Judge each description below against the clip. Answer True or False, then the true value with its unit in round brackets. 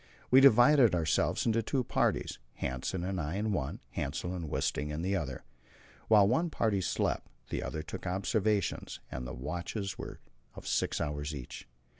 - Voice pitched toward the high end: False (95 Hz)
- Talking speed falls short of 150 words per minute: False (170 wpm)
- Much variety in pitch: True (6.5 semitones)